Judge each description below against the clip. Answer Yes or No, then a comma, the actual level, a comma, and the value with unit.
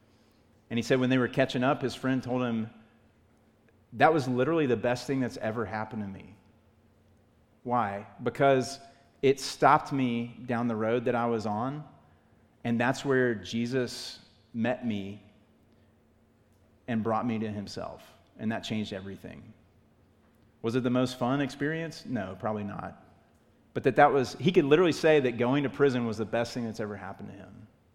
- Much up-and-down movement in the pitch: No, average, 3.0 semitones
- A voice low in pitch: Yes, low, 115 Hz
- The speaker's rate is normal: Yes, average, 170 wpm